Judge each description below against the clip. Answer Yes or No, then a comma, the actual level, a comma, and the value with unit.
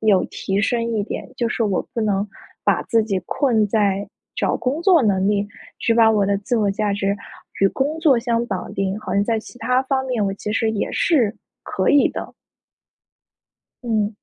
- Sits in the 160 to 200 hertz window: No, high, 220 Hz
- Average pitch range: Yes, average, 3.1 semitones